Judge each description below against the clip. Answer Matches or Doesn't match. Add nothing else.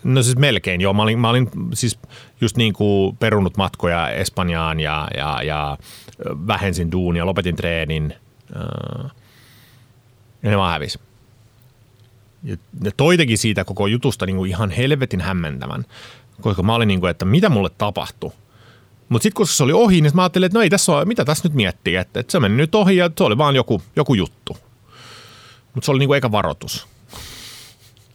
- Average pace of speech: Doesn't match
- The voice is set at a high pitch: Doesn't match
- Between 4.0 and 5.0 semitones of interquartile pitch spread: Matches